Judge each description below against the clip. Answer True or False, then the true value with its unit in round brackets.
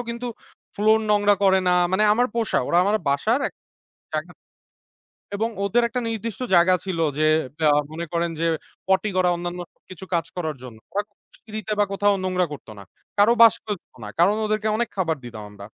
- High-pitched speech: True (195 Hz)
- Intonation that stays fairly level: False (4.1 semitones)